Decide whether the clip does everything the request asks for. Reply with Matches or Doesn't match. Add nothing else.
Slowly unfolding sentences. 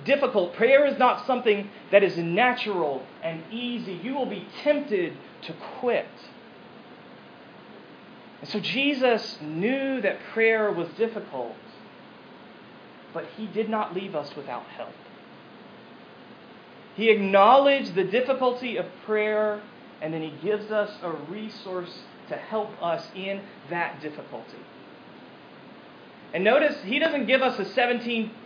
Matches